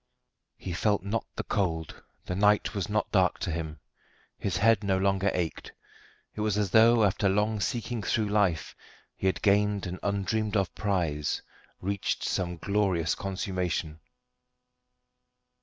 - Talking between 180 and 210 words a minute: No, average, 140 wpm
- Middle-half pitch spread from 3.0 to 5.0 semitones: No, narrow, 2.5 semitones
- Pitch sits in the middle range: No, low, 100 Hz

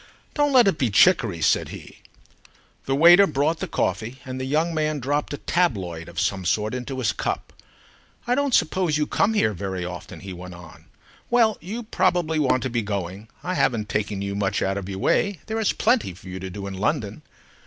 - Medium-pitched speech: No, low, 130 Hz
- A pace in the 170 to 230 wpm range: Yes, fast, 205 wpm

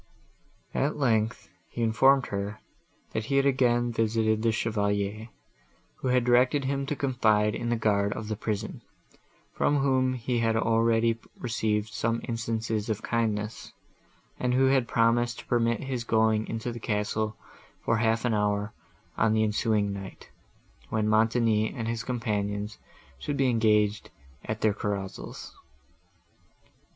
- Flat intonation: Yes, narrow, 2.1 semitones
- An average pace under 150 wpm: Yes, average, 140 wpm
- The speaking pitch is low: Yes, low, 115 Hz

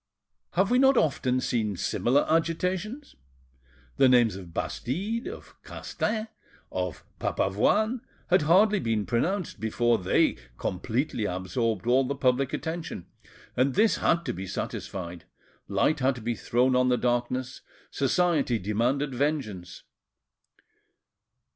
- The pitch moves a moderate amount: No, wide, 6.9 semitones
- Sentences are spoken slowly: Yes, slow, 120 wpm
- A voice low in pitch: Yes, low, 130 Hz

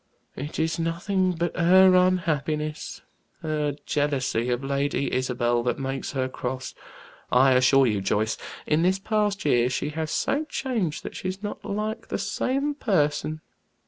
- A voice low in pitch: No, medium, 155 Hz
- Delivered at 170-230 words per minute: No, average, 145 wpm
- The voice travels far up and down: Yes, wide, 5.8 semitones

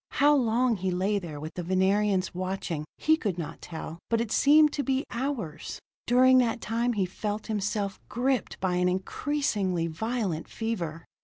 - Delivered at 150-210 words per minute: Yes, average, 165 wpm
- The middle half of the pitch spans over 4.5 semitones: Yes, average, 5.2 semitones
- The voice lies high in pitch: Yes, high, 205 Hz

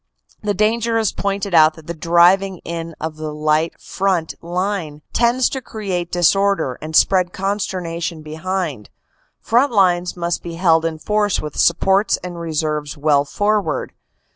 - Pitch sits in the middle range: Yes, medium, 175 Hz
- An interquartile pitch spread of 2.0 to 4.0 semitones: Yes, average, 3.7 semitones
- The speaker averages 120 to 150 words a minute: Yes, average, 145 wpm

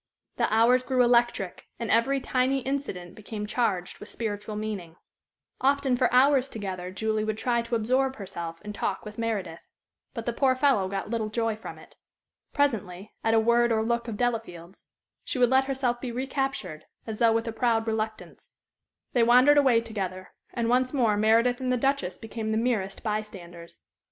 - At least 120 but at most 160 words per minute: No, average, 180 wpm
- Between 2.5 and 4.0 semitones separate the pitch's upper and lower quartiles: Yes, average, 3.1 semitones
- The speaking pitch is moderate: No, high, 230 Hz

